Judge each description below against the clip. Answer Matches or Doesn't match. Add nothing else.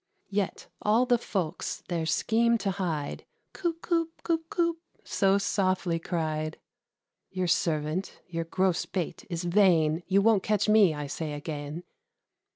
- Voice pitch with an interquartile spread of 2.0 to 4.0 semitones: Doesn't match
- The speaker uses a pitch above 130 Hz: Matches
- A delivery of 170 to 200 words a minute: Doesn't match